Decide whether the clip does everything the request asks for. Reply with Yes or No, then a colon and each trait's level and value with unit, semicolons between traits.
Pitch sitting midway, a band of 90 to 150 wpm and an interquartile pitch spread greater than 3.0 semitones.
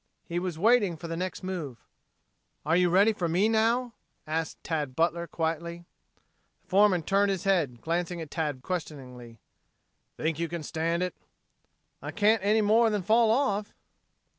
No: medium, 175 Hz; average, 160 wpm; average, 4.0 semitones